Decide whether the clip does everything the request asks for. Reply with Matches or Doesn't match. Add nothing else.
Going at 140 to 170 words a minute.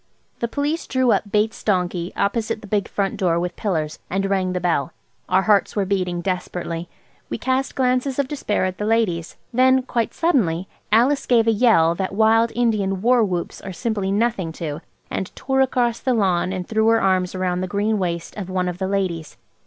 Doesn't match